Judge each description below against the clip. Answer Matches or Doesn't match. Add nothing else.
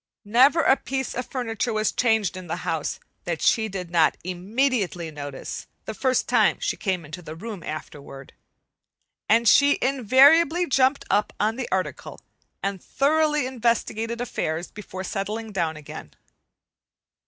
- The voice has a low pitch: Doesn't match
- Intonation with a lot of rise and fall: Matches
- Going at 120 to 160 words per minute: Matches